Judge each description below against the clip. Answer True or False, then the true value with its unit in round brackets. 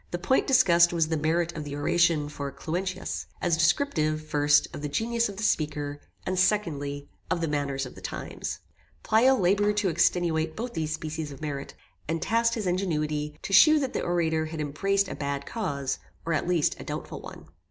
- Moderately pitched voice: True (165 Hz)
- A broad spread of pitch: False (4.4 semitones)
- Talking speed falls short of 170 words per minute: False (195 wpm)